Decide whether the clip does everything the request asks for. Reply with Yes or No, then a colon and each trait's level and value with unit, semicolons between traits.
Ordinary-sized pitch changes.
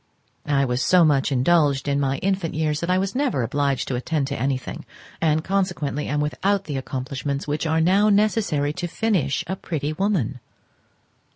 Yes: average, 4.9 semitones